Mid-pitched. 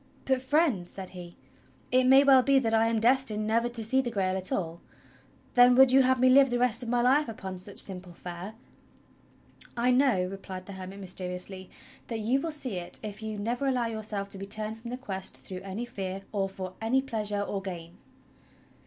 No: high, 220 Hz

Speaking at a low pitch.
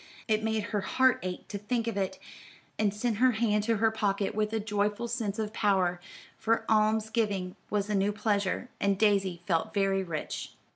No: high, 210 Hz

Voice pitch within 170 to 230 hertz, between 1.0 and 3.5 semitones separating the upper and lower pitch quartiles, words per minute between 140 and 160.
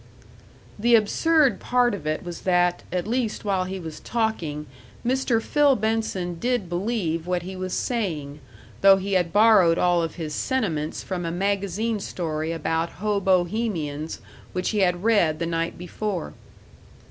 No: medium, 185 Hz; average, 4.6 semitones; average, 150 wpm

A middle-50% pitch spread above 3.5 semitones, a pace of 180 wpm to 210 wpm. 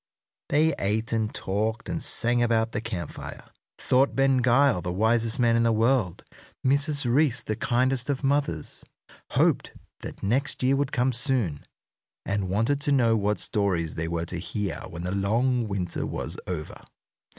No: average, 4.9 semitones; average, 165 wpm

